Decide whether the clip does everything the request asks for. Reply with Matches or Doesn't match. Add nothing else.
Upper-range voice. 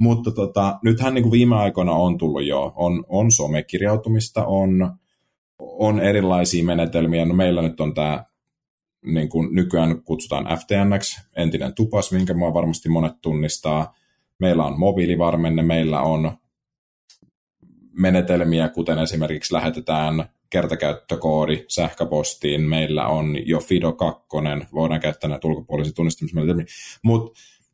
Doesn't match